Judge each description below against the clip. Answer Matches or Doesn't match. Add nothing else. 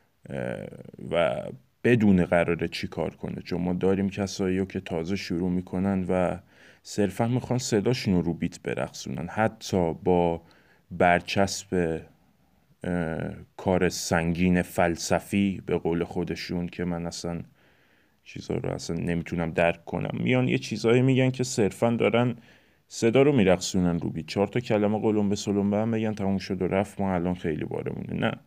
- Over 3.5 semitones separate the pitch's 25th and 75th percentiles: Doesn't match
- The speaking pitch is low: Matches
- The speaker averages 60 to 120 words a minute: Doesn't match